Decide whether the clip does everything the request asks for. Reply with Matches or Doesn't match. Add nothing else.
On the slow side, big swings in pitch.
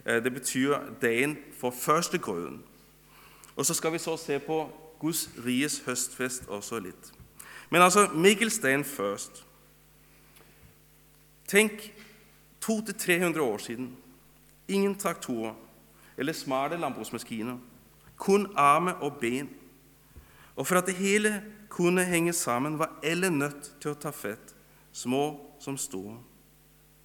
Matches